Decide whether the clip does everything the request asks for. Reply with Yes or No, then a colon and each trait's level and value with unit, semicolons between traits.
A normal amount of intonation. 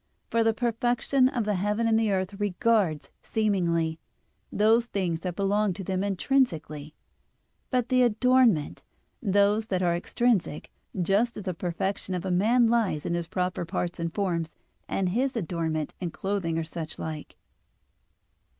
Yes: average, 4.8 semitones